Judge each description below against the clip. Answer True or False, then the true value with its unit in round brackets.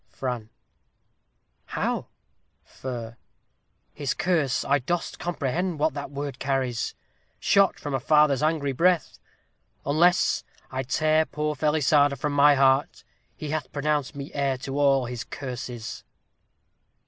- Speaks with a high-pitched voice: False (145 Hz)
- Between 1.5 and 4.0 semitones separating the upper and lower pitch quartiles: True (2.5 semitones)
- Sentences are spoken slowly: True (125 wpm)